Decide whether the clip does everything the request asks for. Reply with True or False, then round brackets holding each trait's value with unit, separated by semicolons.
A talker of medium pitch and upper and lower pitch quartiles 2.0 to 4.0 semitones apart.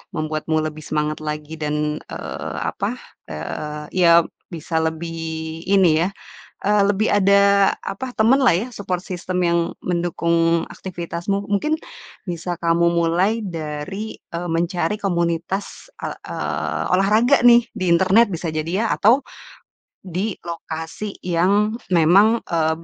True (175 Hz; 3.6 semitones)